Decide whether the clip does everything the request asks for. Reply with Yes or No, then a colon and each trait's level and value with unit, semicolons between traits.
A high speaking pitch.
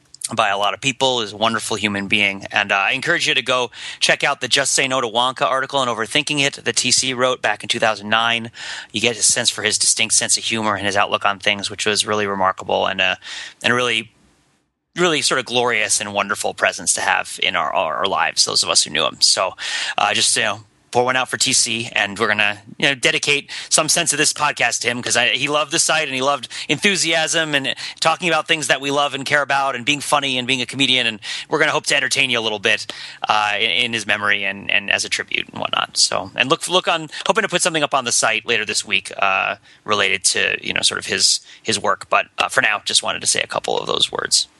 No: low, 125 Hz